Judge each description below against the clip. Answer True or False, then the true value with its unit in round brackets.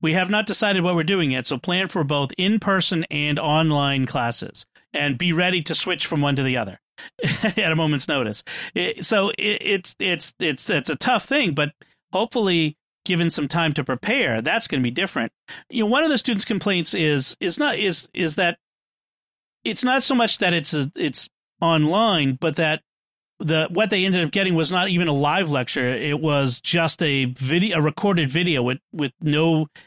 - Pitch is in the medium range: True (165 Hz)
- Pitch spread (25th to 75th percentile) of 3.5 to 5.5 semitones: True (4.8 semitones)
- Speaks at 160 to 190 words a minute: False (200 wpm)